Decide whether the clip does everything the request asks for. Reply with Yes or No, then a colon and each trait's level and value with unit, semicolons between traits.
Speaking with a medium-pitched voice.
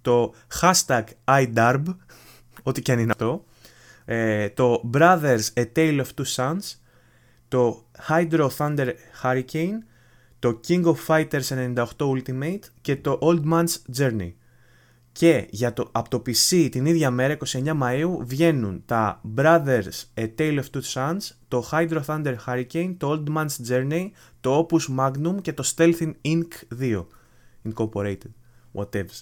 No: low, 130 Hz